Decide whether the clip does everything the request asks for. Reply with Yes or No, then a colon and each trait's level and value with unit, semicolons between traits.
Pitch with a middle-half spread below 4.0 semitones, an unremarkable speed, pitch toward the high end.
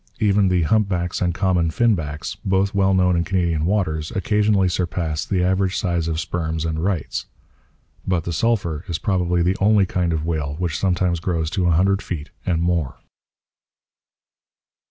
No: average, 2.8 semitones; average, 160 wpm; very low, 90 Hz